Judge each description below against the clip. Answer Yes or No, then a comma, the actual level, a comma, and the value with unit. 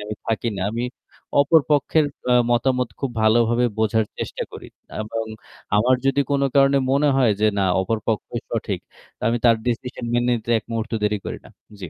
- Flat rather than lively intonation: No, average, 3.3 semitones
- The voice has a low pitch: Yes, low, 120 Hz